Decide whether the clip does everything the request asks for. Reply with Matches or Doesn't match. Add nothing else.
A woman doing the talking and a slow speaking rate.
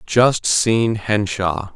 Doesn't match